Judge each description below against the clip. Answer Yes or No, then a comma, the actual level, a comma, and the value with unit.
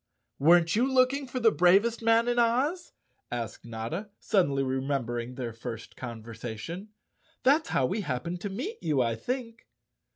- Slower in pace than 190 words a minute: Yes, average, 160 wpm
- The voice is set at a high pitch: No, medium, 175 Hz